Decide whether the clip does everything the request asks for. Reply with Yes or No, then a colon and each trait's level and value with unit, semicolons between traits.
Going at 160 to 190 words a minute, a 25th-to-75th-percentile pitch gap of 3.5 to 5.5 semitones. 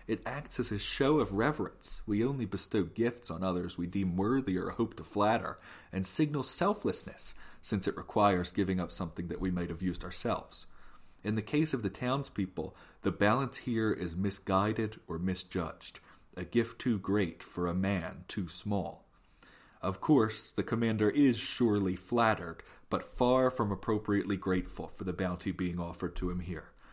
Yes: average, 170 wpm; average, 3.9 semitones